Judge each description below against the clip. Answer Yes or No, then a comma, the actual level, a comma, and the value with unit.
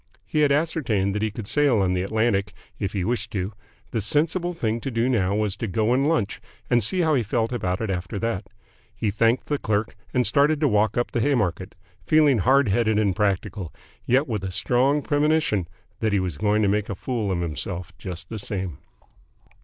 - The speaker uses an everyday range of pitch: Yes, average, 5.0 semitones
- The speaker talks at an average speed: No, fast, 210 wpm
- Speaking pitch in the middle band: No, low, 110 Hz